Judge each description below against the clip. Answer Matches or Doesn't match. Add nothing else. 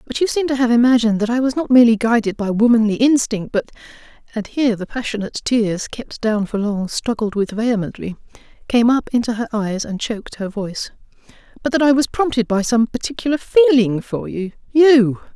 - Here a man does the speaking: Doesn't match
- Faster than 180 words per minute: Doesn't match